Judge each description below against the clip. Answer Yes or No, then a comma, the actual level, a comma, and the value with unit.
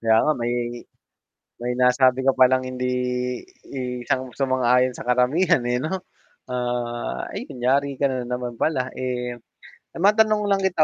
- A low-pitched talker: Yes, low, 125 Hz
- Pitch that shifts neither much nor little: No, narrow, 2.0 semitones